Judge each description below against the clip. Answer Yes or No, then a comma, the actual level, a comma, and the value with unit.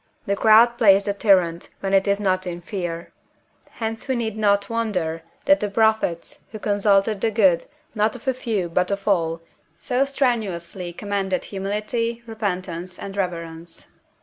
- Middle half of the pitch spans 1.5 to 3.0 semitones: No, average, 3.5 semitones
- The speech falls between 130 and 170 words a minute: Yes, average, 155 wpm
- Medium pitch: No, high, 200 Hz